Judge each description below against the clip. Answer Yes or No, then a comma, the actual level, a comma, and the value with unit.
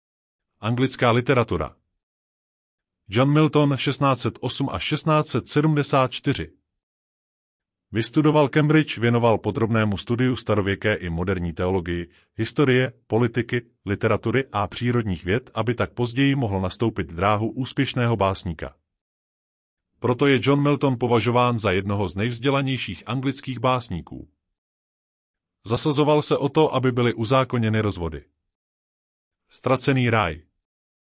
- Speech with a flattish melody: No, wide, 5.9 semitones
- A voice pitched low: Yes, low, 115 Hz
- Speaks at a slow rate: Yes, slow, 100 wpm